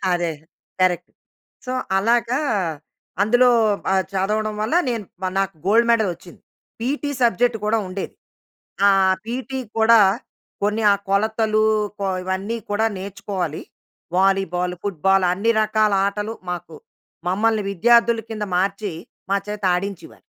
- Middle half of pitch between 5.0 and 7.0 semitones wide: No, average, 2.8 semitones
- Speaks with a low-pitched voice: No, high, 205 Hz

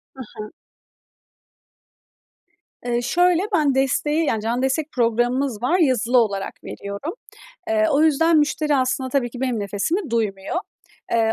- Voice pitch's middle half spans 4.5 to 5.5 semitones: Yes, average, 4.8 semitones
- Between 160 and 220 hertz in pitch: No, very high, 255 Hz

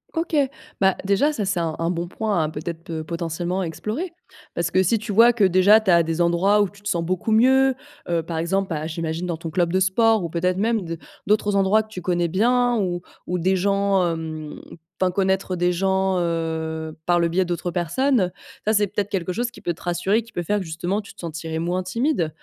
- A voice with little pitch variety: No, average, 3.4 semitones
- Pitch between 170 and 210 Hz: Yes, medium, 185 Hz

